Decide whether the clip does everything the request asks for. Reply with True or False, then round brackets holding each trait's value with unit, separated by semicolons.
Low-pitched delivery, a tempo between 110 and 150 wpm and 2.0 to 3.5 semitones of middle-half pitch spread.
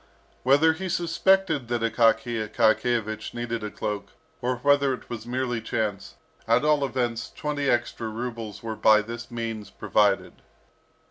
True (120 Hz; 140 wpm; 3.1 semitones)